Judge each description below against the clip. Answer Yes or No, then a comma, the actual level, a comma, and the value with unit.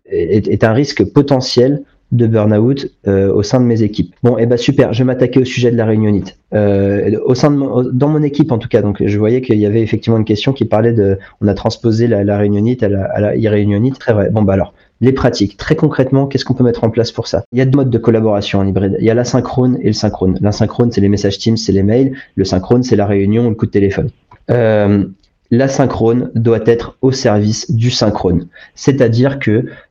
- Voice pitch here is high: No, low, 115 Hz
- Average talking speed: No, fast, 240 wpm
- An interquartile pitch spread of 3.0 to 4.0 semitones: Yes, average, 3.6 semitones